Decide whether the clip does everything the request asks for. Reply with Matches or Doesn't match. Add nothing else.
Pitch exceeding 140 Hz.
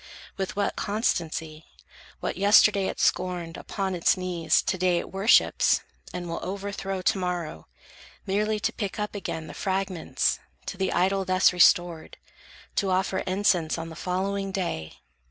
Matches